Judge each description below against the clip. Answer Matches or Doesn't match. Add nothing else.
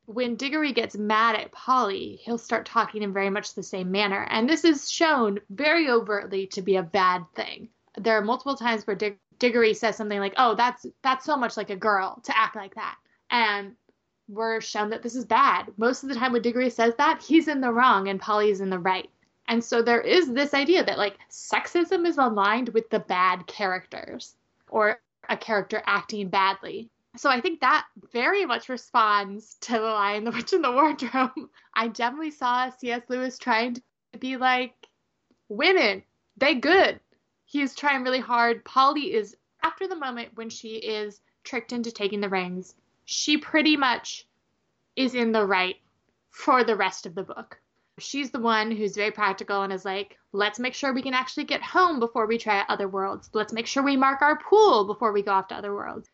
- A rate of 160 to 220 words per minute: Matches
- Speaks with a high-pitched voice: Matches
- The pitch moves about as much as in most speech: Matches